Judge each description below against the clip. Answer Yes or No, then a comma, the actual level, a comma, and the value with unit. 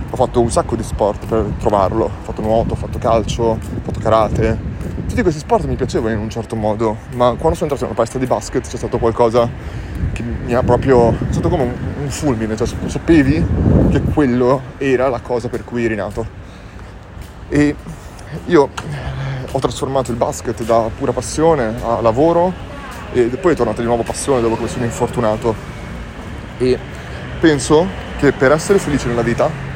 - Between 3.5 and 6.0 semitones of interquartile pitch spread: No, narrow, 2.6 semitones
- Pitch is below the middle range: Yes, low, 120 Hz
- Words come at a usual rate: No, fast, 180 wpm